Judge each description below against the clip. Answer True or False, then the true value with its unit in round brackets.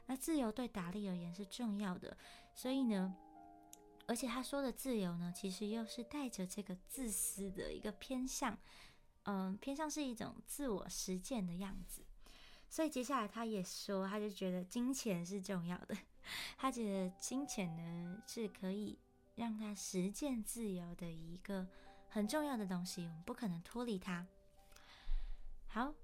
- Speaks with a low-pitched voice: False (200 Hz)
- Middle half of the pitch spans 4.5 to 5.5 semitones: True (4.8 semitones)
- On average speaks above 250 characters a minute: False (235 characters per minute)